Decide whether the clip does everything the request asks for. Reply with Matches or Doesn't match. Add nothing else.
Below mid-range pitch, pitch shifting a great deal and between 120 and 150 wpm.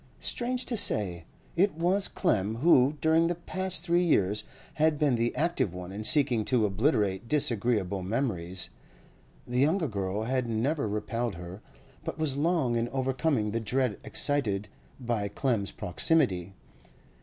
Matches